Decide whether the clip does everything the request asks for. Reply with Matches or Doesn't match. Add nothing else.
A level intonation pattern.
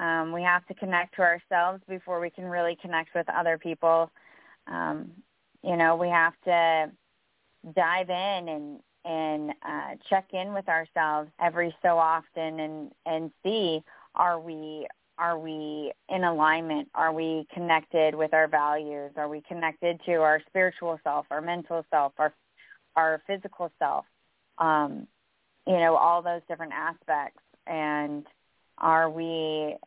Matches